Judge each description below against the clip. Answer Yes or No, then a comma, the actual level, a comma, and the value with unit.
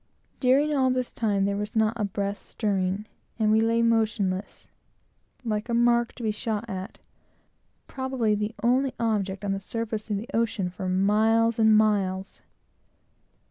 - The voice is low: No, high, 215 Hz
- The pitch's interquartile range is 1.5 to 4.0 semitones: Yes, narrow, 2.5 semitones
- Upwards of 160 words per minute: No, average, 155 wpm